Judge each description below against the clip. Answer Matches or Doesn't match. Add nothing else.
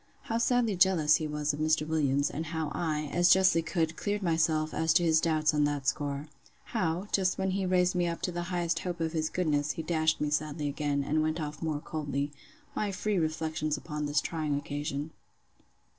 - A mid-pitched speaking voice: Matches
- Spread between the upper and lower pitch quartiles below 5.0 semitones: Matches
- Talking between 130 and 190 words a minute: Doesn't match